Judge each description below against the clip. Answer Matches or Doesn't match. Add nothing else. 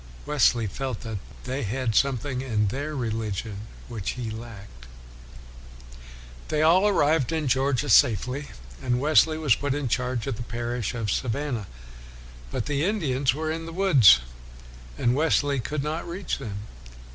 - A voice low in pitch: Matches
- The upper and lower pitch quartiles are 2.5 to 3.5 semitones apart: Doesn't match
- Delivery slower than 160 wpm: Matches